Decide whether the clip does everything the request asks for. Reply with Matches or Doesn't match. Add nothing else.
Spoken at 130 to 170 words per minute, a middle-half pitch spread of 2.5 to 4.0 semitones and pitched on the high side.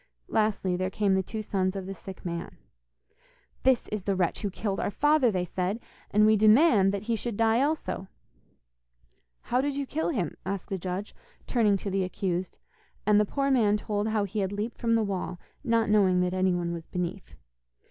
Doesn't match